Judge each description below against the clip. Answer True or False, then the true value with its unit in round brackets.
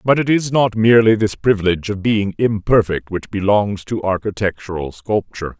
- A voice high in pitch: False (105 Hz)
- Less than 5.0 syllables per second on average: False (5.3 syllables/s)